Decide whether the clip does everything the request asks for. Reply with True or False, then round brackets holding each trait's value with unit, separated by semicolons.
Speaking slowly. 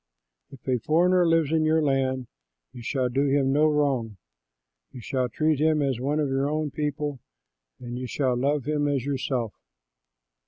False (170 wpm)